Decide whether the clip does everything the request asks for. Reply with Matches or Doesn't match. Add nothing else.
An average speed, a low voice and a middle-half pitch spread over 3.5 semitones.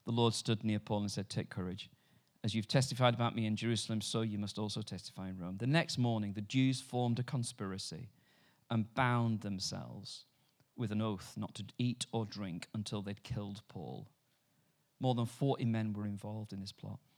Doesn't match